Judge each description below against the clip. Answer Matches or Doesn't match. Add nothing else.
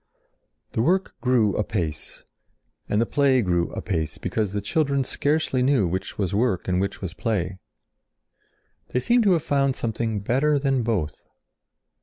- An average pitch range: Doesn't match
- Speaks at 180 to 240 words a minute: Doesn't match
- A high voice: Doesn't match